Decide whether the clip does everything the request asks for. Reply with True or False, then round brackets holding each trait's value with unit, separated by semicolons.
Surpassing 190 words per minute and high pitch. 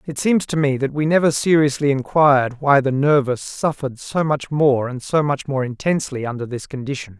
False (200 wpm; 140 Hz)